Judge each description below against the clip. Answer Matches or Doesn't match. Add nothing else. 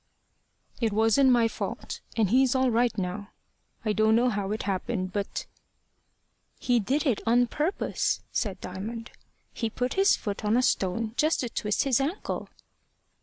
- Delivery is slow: Doesn't match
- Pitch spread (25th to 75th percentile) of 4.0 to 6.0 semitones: Doesn't match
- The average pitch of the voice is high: Matches